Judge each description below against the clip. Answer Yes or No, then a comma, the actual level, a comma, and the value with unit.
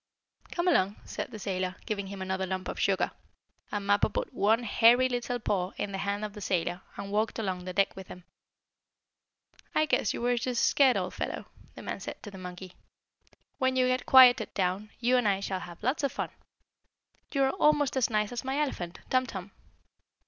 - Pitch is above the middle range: Yes, high, 210 Hz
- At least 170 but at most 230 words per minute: Yes, average, 200 wpm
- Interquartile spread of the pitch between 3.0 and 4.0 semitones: No, average, 5.0 semitones